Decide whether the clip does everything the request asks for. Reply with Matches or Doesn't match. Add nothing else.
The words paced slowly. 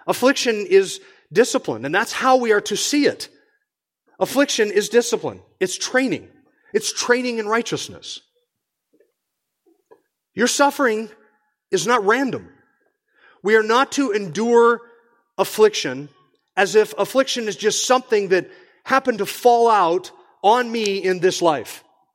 Matches